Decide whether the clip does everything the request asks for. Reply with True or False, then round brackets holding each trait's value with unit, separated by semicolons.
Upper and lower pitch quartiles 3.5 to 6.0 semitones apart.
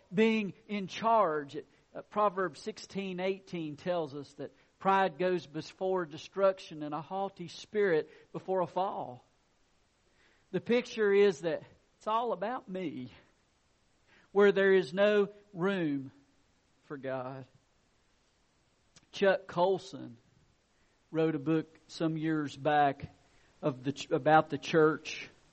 True (4.7 semitones)